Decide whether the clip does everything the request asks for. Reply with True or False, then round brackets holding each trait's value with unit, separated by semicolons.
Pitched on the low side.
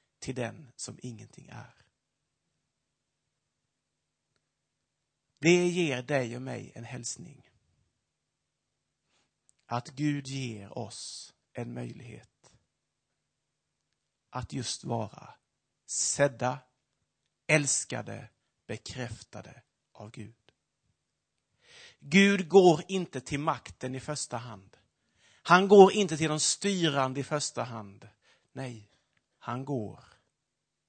True (130 Hz)